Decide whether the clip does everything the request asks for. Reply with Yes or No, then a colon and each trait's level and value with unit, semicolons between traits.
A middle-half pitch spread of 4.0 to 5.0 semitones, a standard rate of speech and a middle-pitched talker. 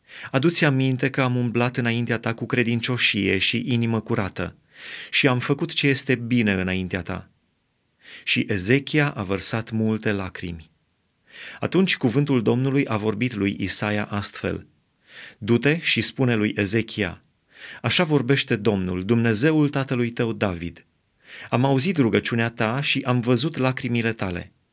No: average, 4.3 semitones; average, 135 wpm; low, 115 Hz